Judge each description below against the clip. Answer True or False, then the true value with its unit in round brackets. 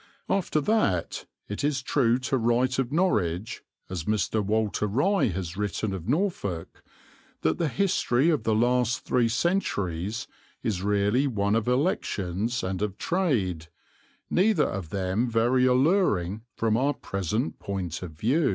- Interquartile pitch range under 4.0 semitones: False (5.6 semitones)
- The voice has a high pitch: False (115 Hz)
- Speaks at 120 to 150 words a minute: True (140 wpm)